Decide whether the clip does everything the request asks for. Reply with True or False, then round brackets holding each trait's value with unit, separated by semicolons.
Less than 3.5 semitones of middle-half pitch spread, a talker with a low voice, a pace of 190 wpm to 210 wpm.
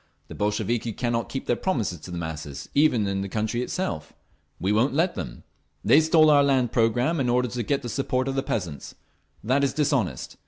False (5.2 semitones; 120 Hz; 200 wpm)